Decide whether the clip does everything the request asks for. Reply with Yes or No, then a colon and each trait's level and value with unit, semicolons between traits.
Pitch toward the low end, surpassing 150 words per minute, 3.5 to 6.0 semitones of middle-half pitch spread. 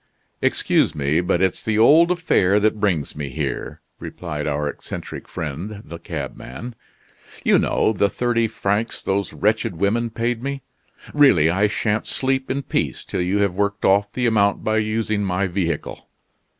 Yes: low, 100 Hz; average, 160 wpm; average, 4.2 semitones